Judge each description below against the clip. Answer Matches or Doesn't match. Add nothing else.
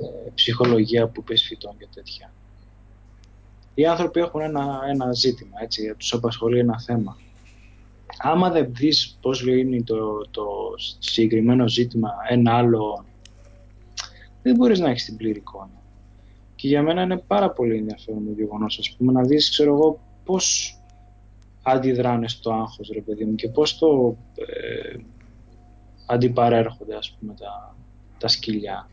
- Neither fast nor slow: Matches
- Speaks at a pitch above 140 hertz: Doesn't match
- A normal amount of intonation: Matches